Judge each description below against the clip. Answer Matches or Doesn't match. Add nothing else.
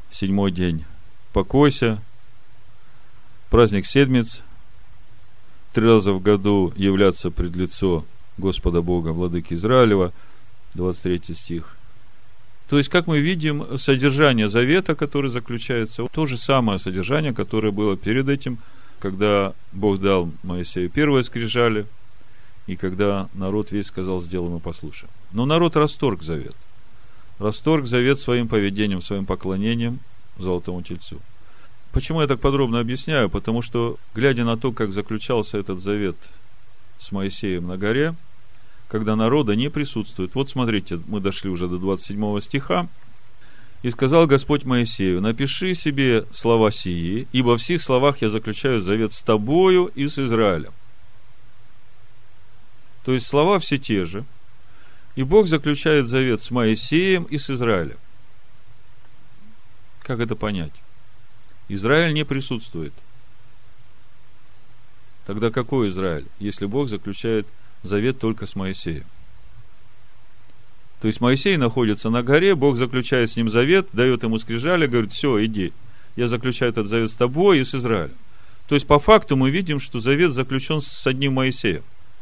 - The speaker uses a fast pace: Doesn't match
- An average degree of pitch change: Matches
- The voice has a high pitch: Doesn't match